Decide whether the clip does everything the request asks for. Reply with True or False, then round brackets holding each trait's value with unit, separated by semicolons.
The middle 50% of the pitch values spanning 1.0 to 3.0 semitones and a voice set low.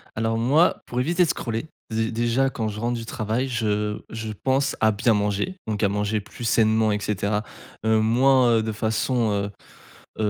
True (2.5 semitones; 110 Hz)